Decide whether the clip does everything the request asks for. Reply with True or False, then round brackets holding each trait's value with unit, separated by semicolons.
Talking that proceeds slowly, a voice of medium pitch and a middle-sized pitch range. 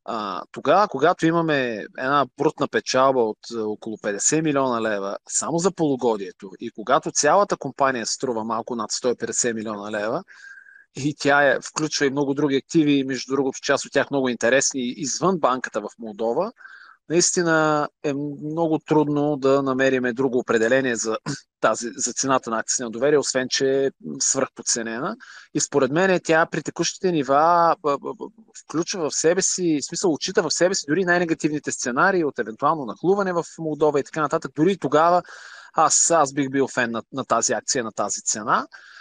False (160 wpm; 145 Hz; 3.8 semitones)